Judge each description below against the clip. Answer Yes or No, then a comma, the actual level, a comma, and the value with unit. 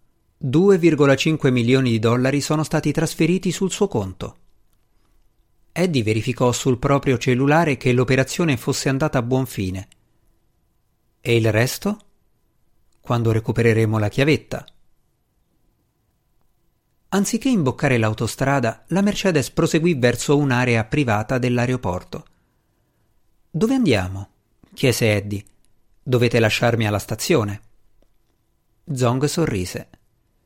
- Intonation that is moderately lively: Yes, average, 4.8 semitones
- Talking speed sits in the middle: No, slow, 95 wpm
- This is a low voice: Yes, low, 125 Hz